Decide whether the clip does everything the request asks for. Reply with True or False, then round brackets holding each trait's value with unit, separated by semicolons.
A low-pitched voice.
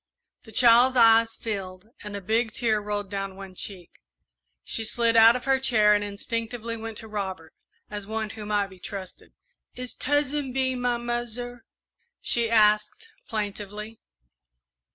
False (220 Hz)